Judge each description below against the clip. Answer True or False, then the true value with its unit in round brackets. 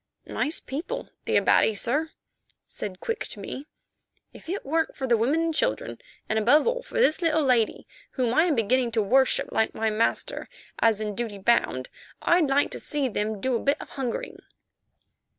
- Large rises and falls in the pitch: True (5.7 semitones)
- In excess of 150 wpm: True (185 wpm)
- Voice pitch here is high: True (260 Hz)